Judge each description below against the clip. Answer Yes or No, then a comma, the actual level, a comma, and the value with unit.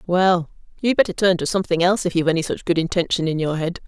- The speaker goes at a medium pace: No, fast, 250 wpm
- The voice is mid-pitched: Yes, medium, 175 Hz